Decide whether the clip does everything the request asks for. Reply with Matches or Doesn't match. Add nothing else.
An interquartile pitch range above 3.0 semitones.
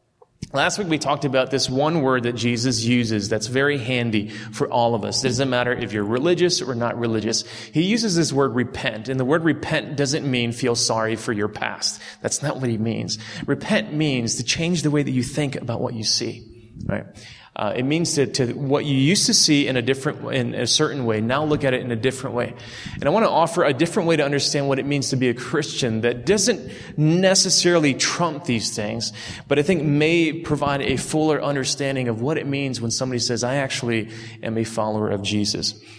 Matches